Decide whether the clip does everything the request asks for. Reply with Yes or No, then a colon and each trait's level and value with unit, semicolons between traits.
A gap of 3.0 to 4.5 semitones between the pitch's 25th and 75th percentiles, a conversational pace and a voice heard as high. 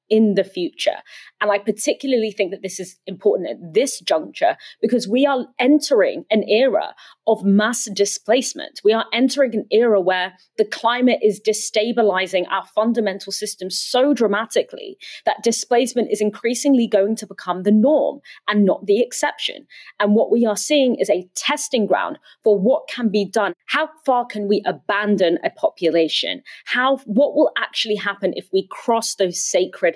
No: average, 5.2 semitones; average, 165 wpm; high, 220 Hz